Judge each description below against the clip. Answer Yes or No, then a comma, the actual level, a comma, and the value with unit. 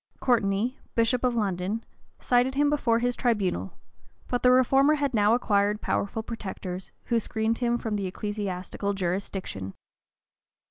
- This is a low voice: No, high, 220 Hz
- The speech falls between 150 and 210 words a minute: No, average, 140 wpm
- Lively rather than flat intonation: No, average, 3.8 semitones